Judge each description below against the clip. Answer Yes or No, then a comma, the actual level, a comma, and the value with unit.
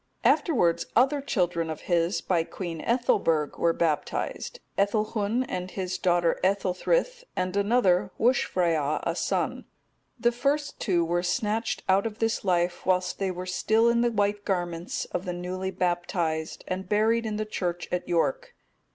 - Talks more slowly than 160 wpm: Yes, average, 150 wpm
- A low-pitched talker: No, medium, 185 Hz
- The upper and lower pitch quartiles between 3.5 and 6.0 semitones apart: Yes, average, 4.2 semitones